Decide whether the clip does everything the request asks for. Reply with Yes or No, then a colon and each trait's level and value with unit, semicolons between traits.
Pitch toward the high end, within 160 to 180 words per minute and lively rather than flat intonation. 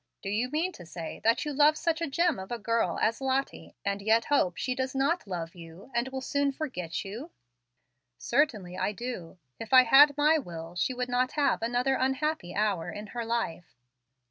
No: high, 245 Hz; average, 195 wpm; wide, 5.8 semitones